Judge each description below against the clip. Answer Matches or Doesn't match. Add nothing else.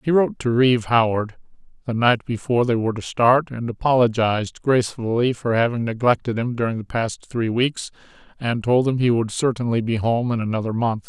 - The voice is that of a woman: Doesn't match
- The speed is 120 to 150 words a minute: Doesn't match